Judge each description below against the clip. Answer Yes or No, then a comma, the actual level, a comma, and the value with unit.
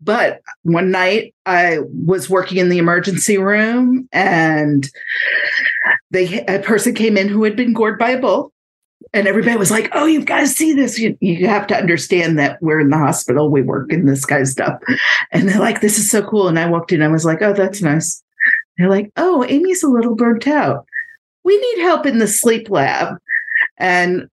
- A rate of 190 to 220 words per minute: Yes, fast, 205 wpm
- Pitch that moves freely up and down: Yes, wide, 6.2 semitones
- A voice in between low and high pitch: No, high, 210 Hz